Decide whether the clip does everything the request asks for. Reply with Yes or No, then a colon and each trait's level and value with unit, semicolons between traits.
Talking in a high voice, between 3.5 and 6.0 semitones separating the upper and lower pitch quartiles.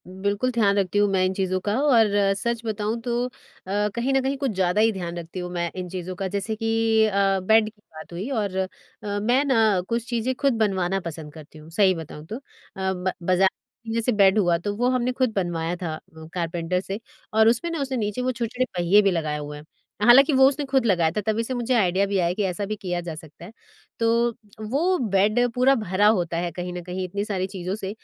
Yes: high, 200 Hz; average, 4.3 semitones